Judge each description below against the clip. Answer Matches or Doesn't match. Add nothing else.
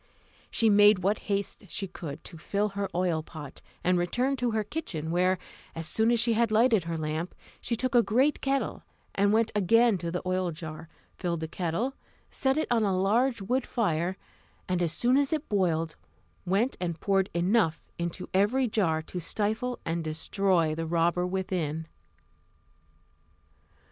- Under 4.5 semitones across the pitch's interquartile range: Doesn't match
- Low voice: Doesn't match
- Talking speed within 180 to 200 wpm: Doesn't match